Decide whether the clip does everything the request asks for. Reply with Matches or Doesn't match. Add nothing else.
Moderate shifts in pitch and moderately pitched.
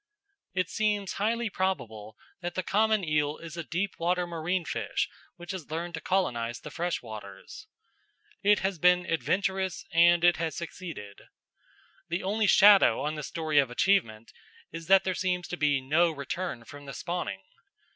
Matches